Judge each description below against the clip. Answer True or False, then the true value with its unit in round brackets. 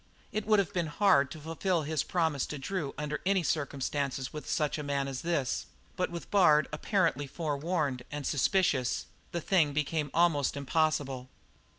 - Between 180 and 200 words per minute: False (165 wpm)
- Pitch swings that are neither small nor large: True (3.5 semitones)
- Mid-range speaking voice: True (150 Hz)